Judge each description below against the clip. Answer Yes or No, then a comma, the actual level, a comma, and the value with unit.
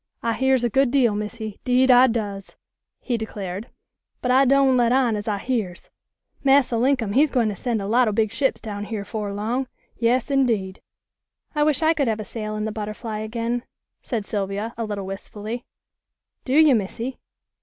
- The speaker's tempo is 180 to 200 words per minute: Yes, average, 185 wpm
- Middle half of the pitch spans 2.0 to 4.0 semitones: Yes, average, 3.5 semitones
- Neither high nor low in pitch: No, high, 230 Hz